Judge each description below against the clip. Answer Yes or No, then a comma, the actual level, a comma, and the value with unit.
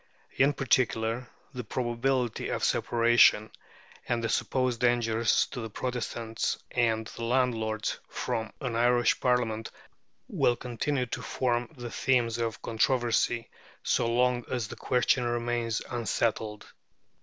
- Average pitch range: No, narrow, 1.5 semitones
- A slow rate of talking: Yes, slow, 120 wpm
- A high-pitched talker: No, low, 120 Hz